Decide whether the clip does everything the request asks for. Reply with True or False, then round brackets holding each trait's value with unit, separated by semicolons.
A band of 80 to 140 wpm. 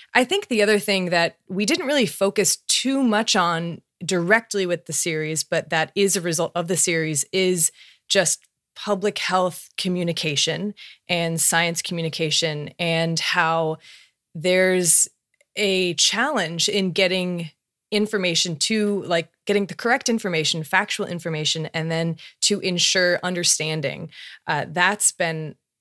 True (135 wpm)